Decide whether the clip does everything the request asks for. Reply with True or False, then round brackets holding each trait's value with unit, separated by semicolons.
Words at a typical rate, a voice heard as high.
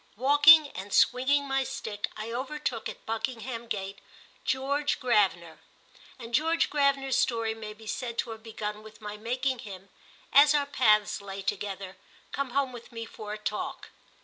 True (160 wpm; 230 Hz)